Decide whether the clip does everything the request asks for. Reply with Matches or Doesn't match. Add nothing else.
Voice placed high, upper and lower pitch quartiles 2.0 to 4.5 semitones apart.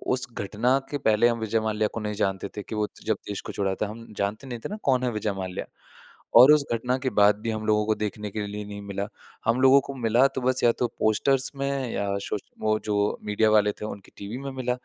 Doesn't match